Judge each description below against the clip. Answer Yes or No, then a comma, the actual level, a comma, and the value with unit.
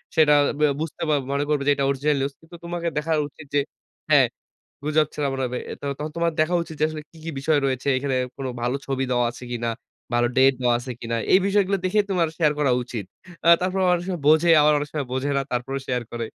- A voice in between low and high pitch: Yes, medium, 145 Hz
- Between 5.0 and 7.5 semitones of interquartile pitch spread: No, average, 3.7 semitones